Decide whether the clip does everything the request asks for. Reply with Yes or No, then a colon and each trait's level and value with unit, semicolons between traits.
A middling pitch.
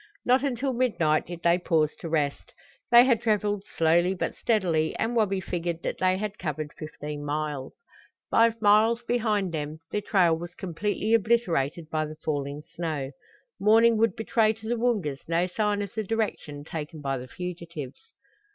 Yes: medium, 180 Hz